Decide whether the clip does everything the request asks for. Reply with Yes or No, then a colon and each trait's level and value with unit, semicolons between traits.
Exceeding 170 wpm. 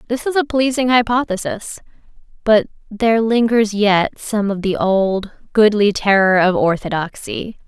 No: slow, 135 wpm